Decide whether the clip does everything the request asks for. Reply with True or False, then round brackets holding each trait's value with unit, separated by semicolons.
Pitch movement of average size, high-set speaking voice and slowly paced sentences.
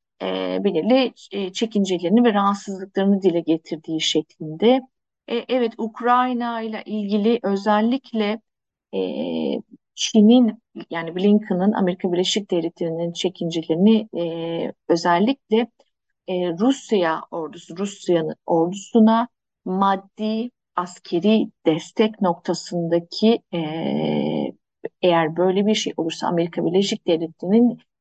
True (4.7 semitones; 195 Hz; 90 wpm)